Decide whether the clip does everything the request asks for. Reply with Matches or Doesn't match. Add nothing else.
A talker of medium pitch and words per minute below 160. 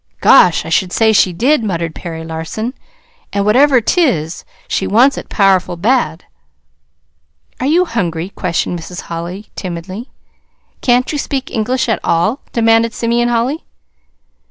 Doesn't match